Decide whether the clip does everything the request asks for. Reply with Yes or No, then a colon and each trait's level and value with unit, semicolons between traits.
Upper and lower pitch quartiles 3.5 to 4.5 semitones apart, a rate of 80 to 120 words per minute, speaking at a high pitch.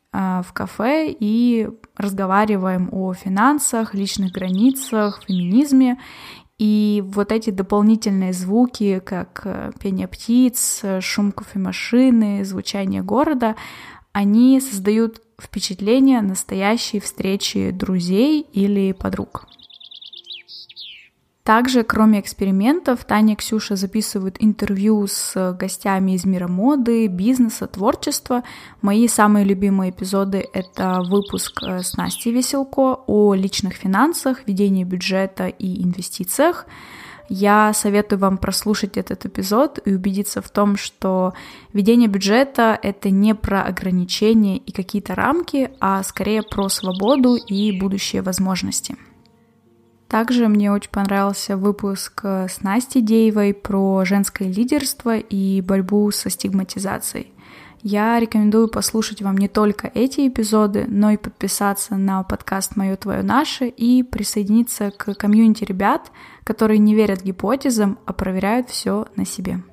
No: average, 2.7 semitones; average, 115 wpm; high, 205 Hz